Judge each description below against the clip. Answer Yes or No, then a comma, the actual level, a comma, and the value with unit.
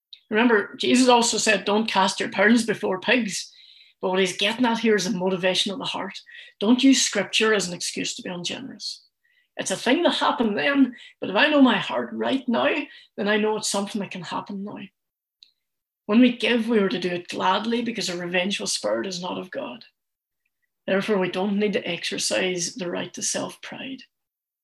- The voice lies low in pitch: No, high, 215 Hz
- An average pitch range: Yes, average, 4.2 semitones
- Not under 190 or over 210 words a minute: Yes, average, 195 wpm